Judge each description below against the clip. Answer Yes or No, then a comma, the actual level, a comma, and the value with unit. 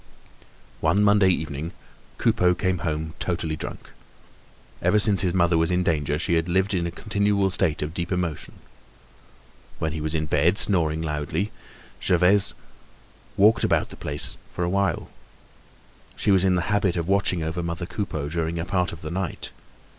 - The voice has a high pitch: No, very low, 85 Hz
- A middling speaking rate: Yes, average, 170 wpm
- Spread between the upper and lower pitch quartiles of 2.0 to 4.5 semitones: Yes, average, 3.1 semitones